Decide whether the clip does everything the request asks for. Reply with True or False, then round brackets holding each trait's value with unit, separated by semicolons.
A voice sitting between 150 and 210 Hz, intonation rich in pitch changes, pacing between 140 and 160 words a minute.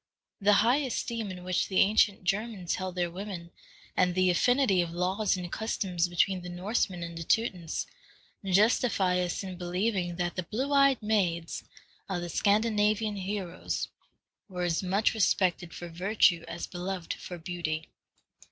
False (185 Hz; 3.0 semitones; 150 wpm)